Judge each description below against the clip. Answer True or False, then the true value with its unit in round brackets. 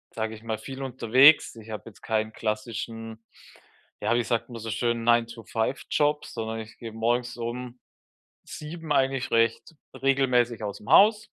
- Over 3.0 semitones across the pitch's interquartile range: False (2.7 semitones)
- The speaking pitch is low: True (115 Hz)